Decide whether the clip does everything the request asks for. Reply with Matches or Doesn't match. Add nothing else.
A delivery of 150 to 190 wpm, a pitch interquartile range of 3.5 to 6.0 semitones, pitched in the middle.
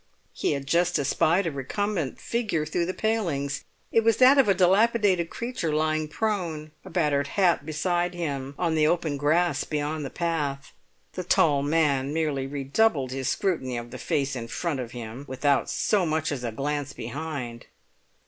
Matches